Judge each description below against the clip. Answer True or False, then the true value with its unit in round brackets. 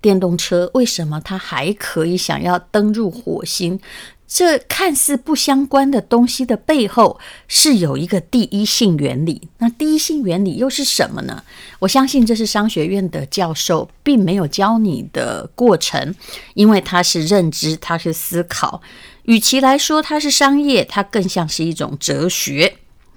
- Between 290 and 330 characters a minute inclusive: False (240 characters per minute)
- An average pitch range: False (7.0 semitones)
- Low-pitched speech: False (205 Hz)